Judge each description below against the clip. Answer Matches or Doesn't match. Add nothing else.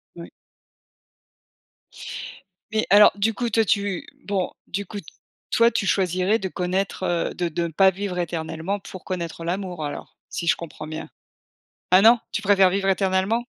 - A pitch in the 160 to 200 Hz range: Matches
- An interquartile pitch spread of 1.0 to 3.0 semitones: Matches